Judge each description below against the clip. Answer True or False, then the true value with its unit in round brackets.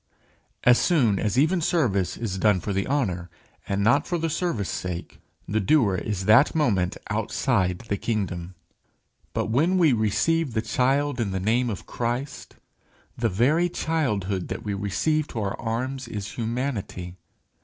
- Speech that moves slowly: False (155 wpm)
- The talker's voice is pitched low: True (115 Hz)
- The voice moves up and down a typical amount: False (6.1 semitones)